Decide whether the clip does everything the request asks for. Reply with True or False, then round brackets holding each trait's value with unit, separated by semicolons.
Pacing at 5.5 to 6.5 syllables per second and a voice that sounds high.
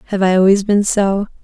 True (5.7 syllables/s; 195 Hz)